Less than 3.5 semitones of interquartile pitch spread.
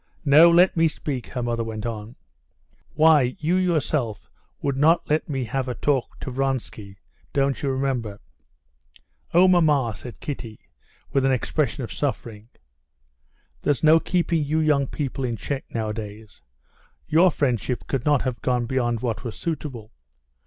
No: average, 4.5 semitones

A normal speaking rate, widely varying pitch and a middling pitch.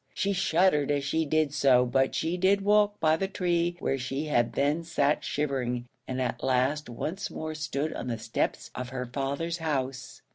No: average, 185 wpm; average, 4.1 semitones; medium, 145 Hz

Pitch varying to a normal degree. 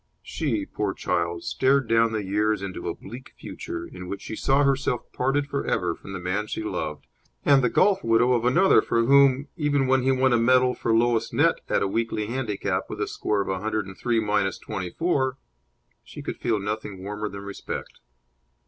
Yes: average, 4.6 semitones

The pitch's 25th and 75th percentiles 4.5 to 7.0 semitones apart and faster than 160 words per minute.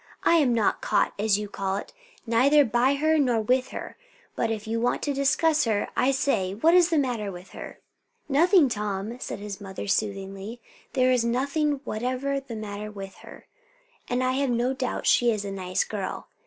Yes: average, 4.8 semitones; average, 190 wpm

